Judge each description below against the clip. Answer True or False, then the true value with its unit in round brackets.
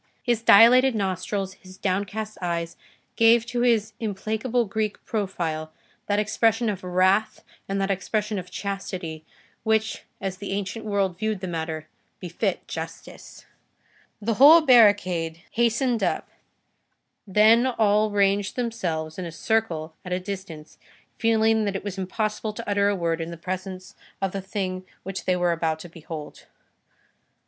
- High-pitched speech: True (200 Hz)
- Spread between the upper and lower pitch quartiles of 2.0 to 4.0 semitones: True (3.3 semitones)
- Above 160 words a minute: False (145 wpm)